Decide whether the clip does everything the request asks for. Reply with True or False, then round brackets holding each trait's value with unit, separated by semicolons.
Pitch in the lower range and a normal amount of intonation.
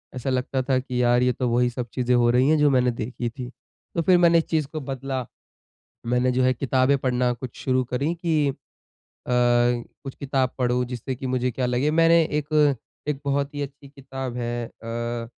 False (130 Hz; 2.3 semitones)